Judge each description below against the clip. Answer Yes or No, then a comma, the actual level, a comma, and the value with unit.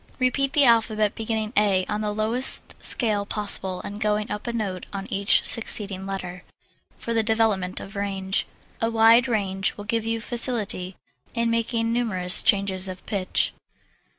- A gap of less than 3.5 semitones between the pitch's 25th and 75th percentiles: Yes, average, 2.7 semitones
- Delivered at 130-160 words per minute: Yes, average, 155 wpm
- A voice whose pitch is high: Yes, high, 210 Hz